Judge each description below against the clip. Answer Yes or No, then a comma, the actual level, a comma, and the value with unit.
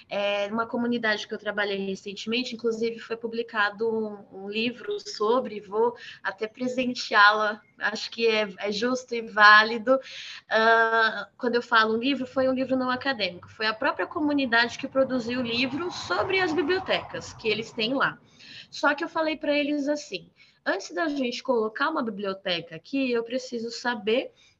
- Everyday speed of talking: Yes, average, 165 wpm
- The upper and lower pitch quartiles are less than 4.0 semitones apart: Yes, average, 3.6 semitones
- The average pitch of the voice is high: Yes, high, 235 Hz